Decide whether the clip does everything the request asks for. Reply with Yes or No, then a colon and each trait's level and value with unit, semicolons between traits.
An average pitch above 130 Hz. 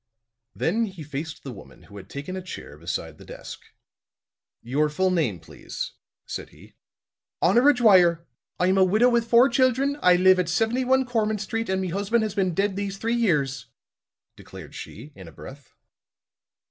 Yes: high, 190 Hz